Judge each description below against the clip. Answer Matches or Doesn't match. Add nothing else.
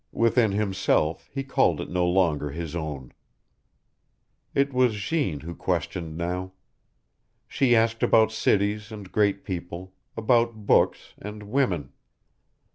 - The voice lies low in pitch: Matches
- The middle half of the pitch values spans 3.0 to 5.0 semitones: Matches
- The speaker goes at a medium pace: Doesn't match